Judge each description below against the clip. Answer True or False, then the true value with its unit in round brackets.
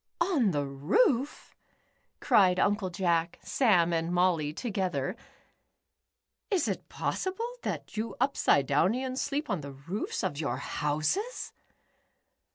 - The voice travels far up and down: True (8.1 semitones)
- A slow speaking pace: True (115 wpm)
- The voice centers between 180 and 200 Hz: True (185 Hz)